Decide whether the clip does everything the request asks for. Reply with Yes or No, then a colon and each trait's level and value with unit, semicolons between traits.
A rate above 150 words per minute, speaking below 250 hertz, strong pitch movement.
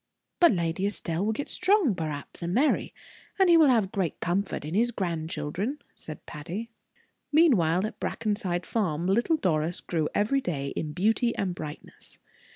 Yes: average, 160 wpm; high, 190 Hz; wide, 6.1 semitones